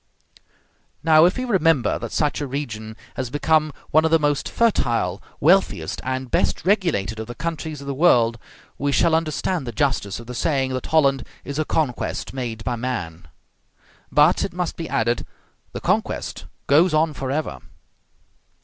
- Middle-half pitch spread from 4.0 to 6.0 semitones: Yes, average, 4.9 semitones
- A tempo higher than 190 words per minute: No, average, 165 wpm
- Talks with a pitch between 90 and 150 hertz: Yes, medium, 140 Hz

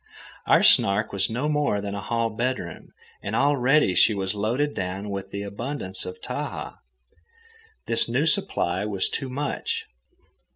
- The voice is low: Yes, low, 110 Hz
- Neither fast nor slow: Yes, average, 150 wpm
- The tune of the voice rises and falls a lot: Yes, wide, 6.0 semitones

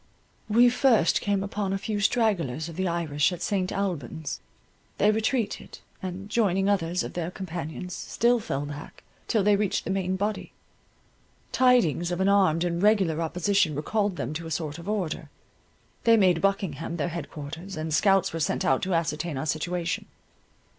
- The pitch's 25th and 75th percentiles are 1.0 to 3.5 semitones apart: No, average, 3.9 semitones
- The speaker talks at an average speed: Yes, average, 170 wpm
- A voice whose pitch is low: No, medium, 180 Hz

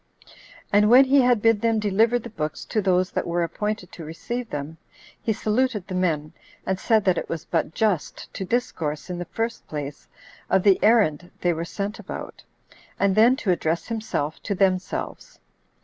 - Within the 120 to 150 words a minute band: No, average, 180 wpm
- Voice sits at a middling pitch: No, high, 195 Hz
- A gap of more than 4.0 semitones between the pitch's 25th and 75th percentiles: Yes, average, 4.9 semitones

